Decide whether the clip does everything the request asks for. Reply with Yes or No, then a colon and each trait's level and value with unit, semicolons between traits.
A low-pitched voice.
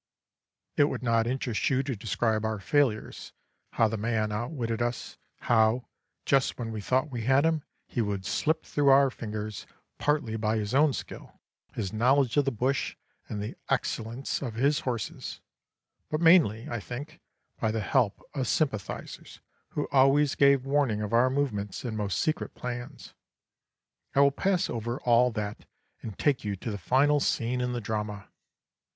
Yes: low, 120 Hz